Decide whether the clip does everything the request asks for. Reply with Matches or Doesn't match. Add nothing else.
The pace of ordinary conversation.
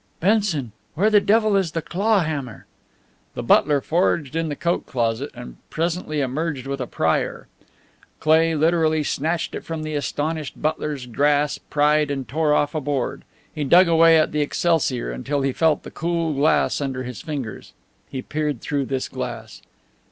Matches